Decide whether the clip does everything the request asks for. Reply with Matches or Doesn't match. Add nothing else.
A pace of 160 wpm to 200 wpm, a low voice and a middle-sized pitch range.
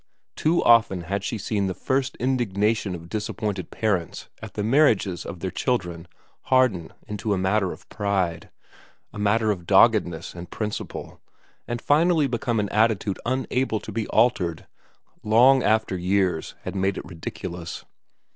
Doesn't match